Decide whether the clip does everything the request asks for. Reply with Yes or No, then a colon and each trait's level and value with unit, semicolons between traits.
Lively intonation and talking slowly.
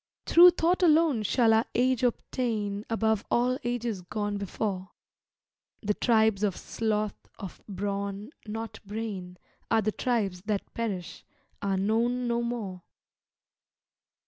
No: average, 3.0 semitones; slow, 120 wpm